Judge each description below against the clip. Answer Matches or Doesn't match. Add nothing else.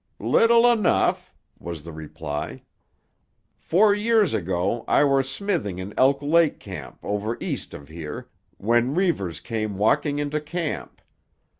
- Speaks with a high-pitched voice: Doesn't match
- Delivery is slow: Matches